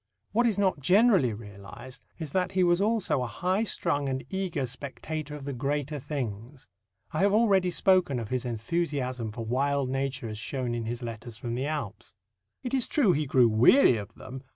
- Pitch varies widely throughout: Yes, wide, 6.8 semitones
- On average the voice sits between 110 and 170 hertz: Yes, medium, 140 Hz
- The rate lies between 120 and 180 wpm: No, average, 190 wpm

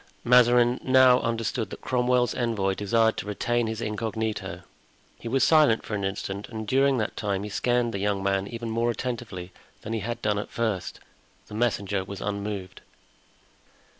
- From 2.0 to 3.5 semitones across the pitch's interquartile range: Yes, average, 2.9 semitones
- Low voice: Yes, low, 110 Hz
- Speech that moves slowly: No, average, 165 wpm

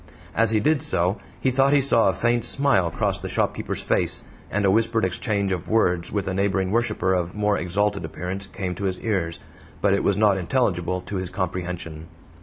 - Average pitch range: Yes, average, 3.6 semitones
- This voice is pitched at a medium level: No, low, 100 Hz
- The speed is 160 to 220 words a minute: Yes, average, 200 wpm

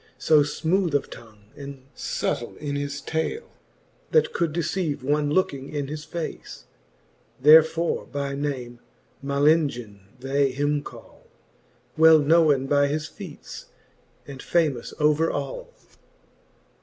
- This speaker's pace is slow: Yes, slow, 120 wpm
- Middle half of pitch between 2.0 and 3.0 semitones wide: Yes, narrow, 2.4 semitones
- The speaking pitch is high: No, medium, 145 Hz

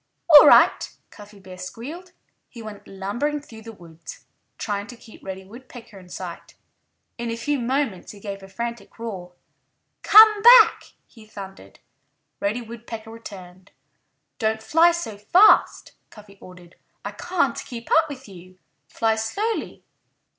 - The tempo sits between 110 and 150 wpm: Yes, average, 140 wpm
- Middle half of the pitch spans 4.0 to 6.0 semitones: Yes, average, 4.8 semitones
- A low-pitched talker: No, high, 220 Hz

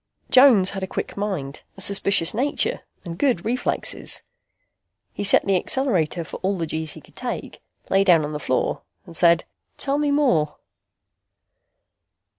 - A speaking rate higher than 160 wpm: No, average, 155 wpm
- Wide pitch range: Yes, wide, 6.0 semitones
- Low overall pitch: No, high, 190 Hz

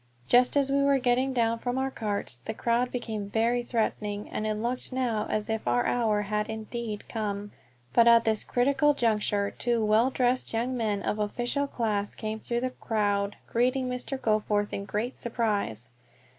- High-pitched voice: Yes, high, 225 Hz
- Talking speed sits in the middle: Yes, average, 175 wpm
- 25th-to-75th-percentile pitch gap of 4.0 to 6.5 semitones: No, average, 2.8 semitones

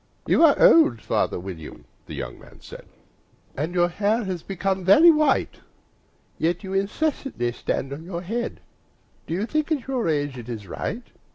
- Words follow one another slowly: No, average, 175 wpm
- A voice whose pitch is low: No, medium, 185 Hz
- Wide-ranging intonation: Yes, wide, 8.5 semitones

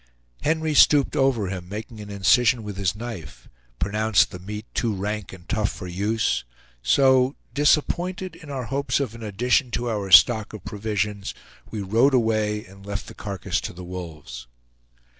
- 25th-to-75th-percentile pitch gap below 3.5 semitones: No, average, 4.2 semitones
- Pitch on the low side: Yes, low, 105 Hz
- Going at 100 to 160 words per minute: No, average, 170 wpm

